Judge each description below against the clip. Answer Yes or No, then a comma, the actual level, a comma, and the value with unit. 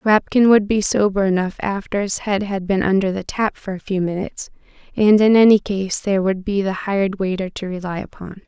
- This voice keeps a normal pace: No, fast, 210 wpm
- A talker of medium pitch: No, high, 195 Hz